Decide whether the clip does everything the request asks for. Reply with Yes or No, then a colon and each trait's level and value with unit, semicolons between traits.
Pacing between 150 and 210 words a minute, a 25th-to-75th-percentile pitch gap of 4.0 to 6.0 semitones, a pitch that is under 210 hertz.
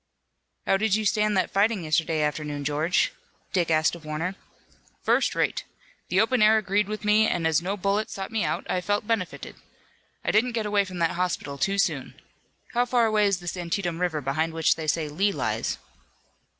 Yes: average, 190 wpm; average, 4.5 semitones; medium, 185 Hz